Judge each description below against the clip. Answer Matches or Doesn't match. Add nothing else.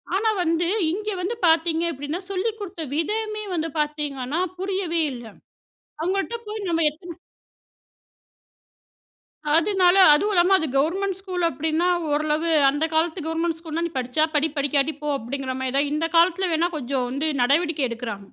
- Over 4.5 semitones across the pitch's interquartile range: Doesn't match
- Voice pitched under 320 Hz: Doesn't match